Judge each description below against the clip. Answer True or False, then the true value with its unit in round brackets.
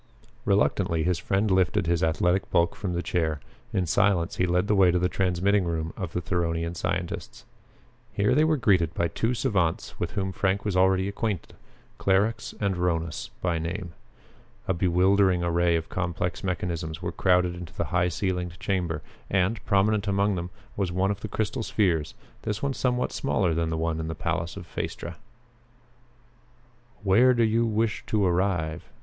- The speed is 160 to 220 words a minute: True (175 wpm)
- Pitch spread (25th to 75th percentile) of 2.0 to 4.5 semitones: True (2.8 semitones)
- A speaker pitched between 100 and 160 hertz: False (90 Hz)